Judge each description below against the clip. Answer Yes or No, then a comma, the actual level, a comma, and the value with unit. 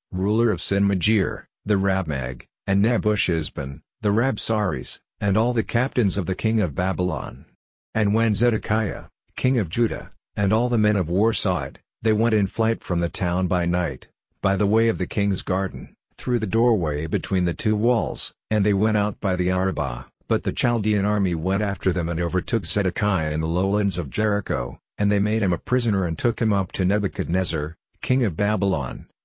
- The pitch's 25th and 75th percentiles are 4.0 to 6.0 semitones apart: No, average, 3.3 semitones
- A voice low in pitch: Yes, low, 100 Hz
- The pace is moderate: Yes, average, 190 wpm